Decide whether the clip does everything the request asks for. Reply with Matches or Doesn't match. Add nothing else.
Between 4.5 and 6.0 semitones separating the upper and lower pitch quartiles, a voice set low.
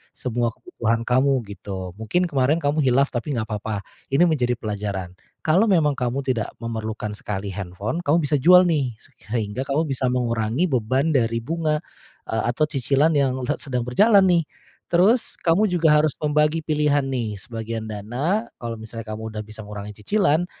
Matches